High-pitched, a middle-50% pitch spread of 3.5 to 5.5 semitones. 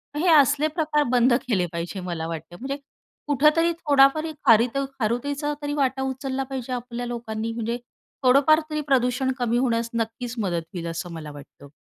Yes: very high, 250 Hz; average, 4.2 semitones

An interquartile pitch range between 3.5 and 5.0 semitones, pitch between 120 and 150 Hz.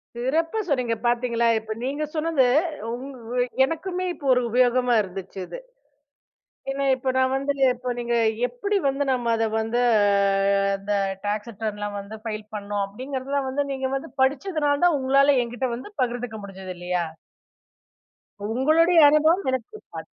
No: average, 3.8 semitones; very high, 255 Hz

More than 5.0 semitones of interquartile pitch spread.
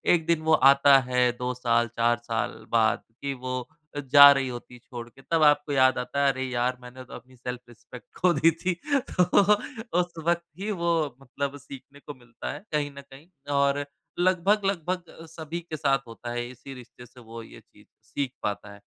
No: average, 4.1 semitones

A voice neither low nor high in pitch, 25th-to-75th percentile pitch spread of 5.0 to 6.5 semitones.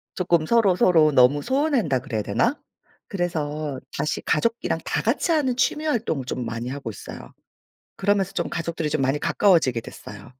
No: medium, 160 Hz; wide, 7.4 semitones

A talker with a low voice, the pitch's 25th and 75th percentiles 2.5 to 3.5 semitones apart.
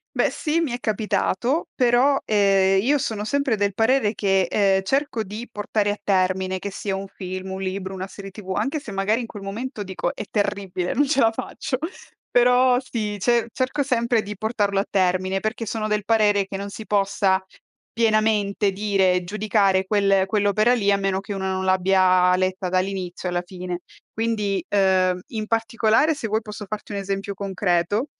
No: high, 205 Hz; average, 2.8 semitones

